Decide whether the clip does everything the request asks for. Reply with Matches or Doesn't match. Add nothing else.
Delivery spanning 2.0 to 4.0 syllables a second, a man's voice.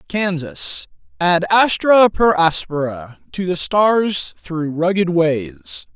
Matches